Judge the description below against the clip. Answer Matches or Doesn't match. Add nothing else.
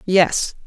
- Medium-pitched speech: Matches